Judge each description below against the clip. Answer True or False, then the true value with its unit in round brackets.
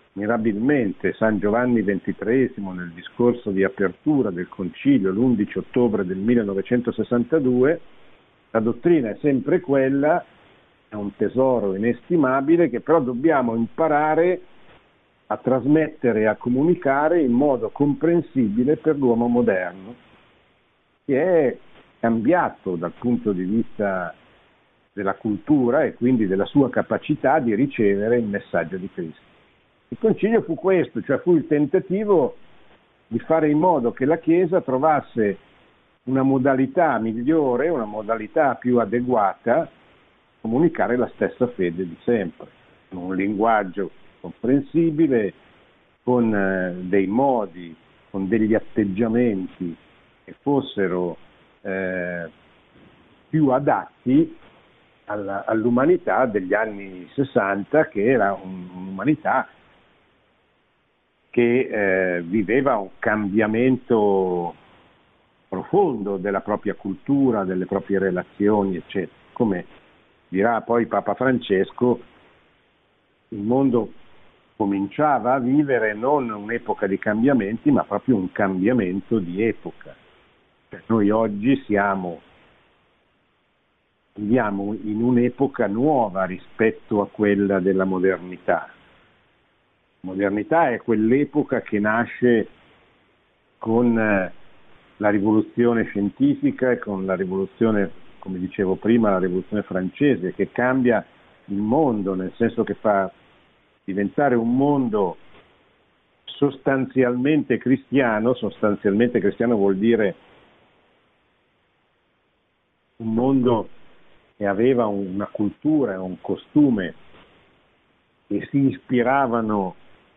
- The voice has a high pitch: False (115 Hz)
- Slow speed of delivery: True (100 wpm)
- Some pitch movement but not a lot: True (4.9 semitones)